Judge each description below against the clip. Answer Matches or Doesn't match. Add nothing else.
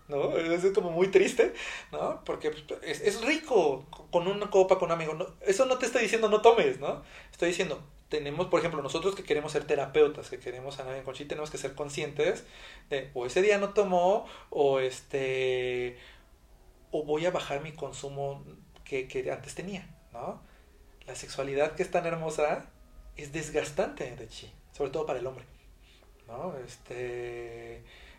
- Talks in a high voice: Doesn't match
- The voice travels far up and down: Matches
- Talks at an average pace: Matches